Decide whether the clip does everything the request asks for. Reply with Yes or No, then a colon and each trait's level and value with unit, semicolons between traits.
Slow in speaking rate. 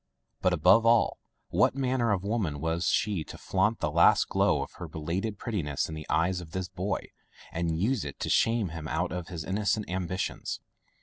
No: average, 190 wpm